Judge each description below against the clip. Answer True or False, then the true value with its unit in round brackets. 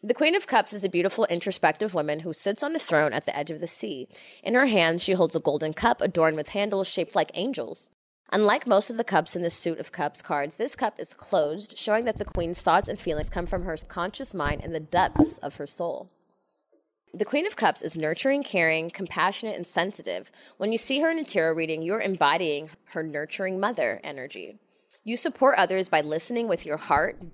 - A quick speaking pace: True (215 wpm)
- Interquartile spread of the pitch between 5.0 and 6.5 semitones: True (5.3 semitones)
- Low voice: False (185 Hz)